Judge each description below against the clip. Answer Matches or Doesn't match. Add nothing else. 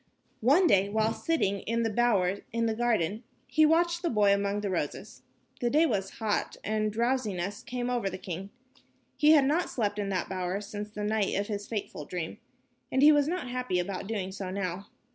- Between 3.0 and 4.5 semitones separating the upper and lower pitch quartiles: Matches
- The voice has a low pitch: Doesn't match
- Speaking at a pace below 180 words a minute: Doesn't match